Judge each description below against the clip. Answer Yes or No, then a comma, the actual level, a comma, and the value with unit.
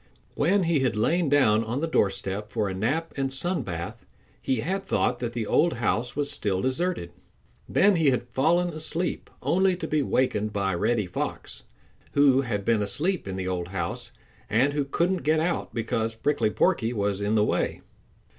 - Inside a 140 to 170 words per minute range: No, average, 185 wpm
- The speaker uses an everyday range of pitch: No, wide, 7.3 semitones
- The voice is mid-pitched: No, low, 125 Hz